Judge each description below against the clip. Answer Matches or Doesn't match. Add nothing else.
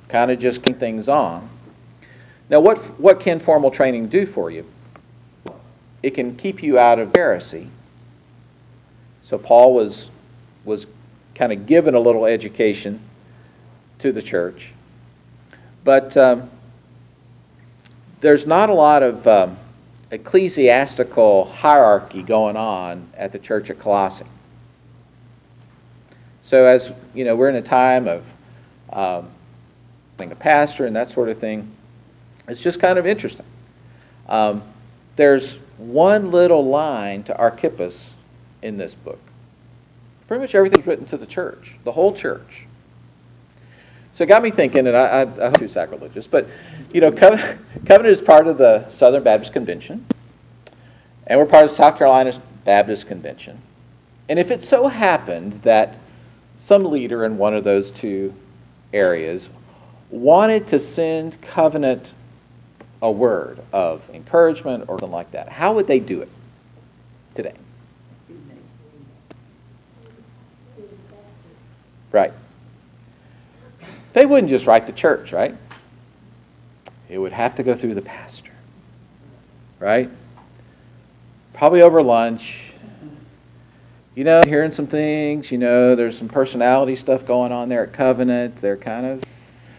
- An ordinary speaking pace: Doesn't match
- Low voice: Matches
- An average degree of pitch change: Doesn't match